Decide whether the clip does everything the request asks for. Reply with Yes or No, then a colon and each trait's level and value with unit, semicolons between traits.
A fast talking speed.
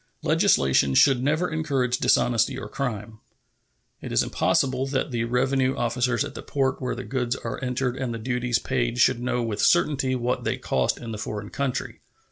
No: average, 180 wpm